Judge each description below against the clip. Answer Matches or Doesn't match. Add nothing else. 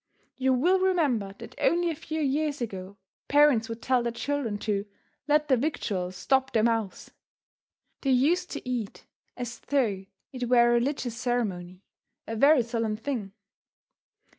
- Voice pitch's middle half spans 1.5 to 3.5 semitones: Doesn't match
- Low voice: Doesn't match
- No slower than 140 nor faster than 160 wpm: Matches